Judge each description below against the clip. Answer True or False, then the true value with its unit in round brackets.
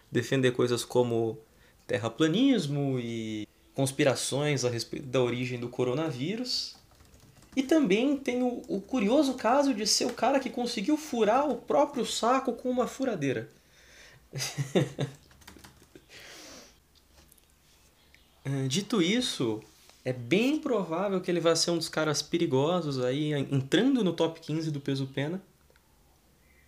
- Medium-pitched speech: True (150 Hz)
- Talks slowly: True (115 wpm)